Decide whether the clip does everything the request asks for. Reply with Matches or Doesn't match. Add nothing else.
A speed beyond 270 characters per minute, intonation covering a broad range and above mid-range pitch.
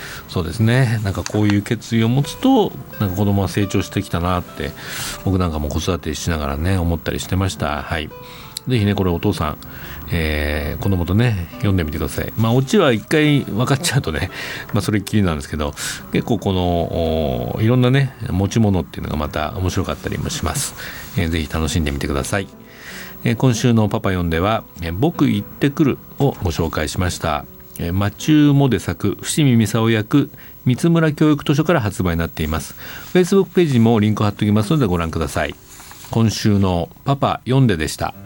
Doesn't match